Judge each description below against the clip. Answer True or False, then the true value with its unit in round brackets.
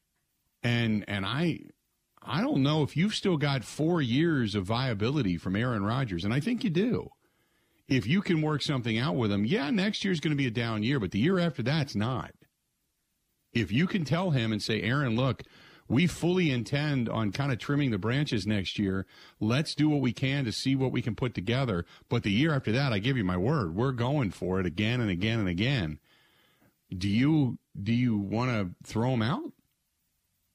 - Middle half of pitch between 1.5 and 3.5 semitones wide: False (5.6 semitones)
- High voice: False (125 Hz)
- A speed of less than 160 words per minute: False (205 wpm)